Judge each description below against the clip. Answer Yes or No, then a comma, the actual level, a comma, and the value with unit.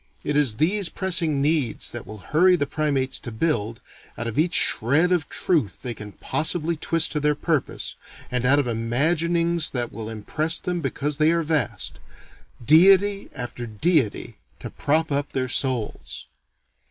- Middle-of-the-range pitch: Yes, medium, 150 Hz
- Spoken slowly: No, average, 160 wpm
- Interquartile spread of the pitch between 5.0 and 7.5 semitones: Yes, wide, 5.4 semitones